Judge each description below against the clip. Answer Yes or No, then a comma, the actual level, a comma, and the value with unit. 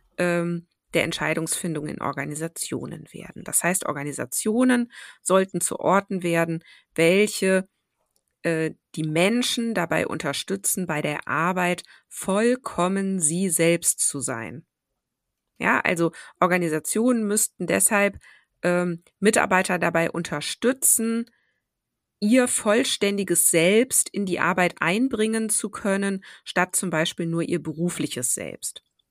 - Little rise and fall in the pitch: No, average, 3.6 semitones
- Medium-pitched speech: Yes, medium, 180 Hz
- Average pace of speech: No, slow, 100 wpm